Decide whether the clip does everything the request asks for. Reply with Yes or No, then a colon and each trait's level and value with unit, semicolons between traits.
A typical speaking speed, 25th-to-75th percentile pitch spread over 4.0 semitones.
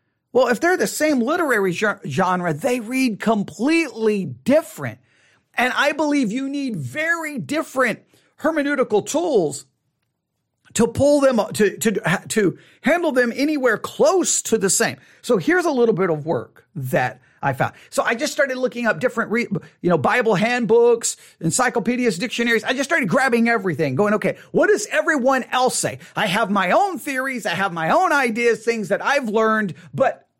Yes: average, 165 wpm; average, 4.8 semitones